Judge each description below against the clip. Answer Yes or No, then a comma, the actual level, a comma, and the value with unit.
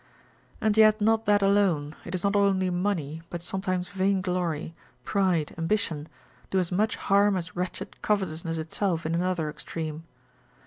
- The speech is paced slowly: No, average, 145 wpm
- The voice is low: No, medium, 185 Hz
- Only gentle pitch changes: No, average, 3.3 semitones